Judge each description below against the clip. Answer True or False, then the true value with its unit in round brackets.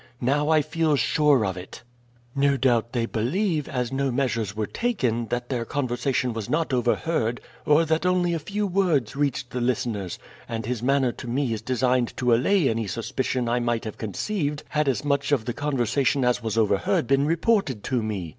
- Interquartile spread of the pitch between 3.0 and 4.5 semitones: True (4.1 semitones)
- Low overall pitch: True (130 Hz)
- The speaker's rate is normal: True (190 wpm)